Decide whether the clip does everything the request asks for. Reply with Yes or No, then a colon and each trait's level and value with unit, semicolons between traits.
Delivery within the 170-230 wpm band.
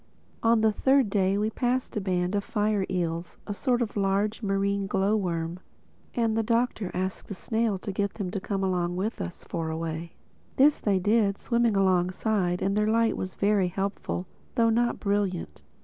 Yes: average, 180 wpm